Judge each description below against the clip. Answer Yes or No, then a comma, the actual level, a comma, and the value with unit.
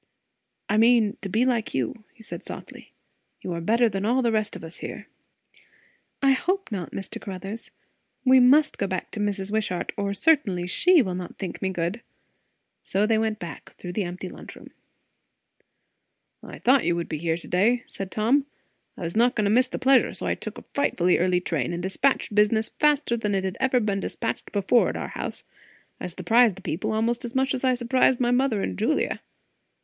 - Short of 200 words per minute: No, fast, 205 wpm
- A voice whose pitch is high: Yes, high, 215 Hz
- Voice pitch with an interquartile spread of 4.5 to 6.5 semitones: Yes, average, 4.9 semitones